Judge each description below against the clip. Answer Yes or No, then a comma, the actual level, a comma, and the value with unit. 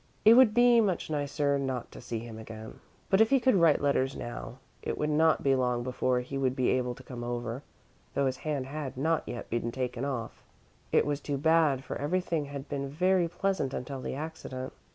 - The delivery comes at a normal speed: No, fast, 210 wpm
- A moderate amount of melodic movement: Yes, average, 4.1 semitones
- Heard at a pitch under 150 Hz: Yes, medium, 140 Hz